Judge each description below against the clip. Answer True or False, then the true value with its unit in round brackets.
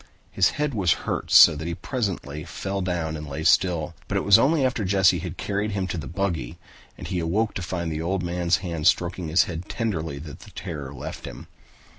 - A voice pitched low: True (90 Hz)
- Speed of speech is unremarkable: False (210 wpm)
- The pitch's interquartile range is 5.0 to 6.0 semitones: False (3.4 semitones)